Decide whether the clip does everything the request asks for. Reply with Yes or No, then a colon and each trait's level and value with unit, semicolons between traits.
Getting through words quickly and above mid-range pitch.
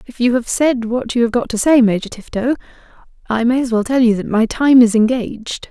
Yes: fast, 240 wpm; high, 235 Hz